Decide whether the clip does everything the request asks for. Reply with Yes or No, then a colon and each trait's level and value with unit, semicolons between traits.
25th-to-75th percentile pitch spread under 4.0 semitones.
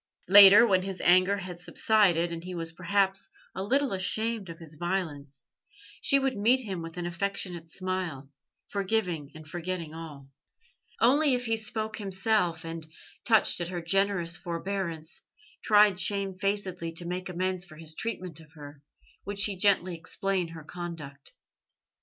Yes: average, 3.3 semitones